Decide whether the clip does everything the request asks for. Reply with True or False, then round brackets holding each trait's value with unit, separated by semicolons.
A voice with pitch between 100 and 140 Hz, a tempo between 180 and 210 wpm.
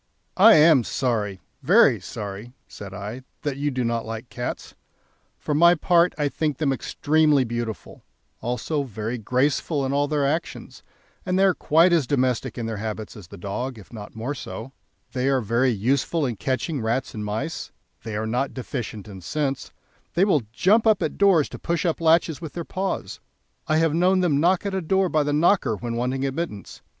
True (135 Hz; 190 wpm)